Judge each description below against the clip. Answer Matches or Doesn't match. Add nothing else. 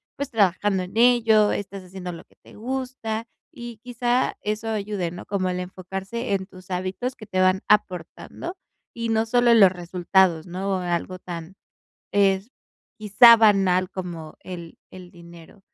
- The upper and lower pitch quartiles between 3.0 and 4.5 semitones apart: Matches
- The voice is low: Doesn't match